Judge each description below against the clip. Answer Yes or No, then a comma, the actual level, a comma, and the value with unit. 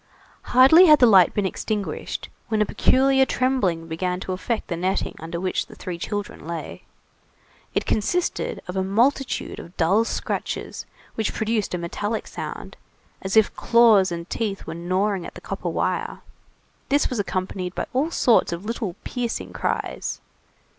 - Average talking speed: Yes, average, 160 wpm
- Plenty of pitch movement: No, average, 4.6 semitones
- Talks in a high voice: Yes, high, 205 Hz